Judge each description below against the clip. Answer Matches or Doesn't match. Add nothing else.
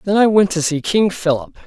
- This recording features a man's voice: Matches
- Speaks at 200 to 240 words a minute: Doesn't match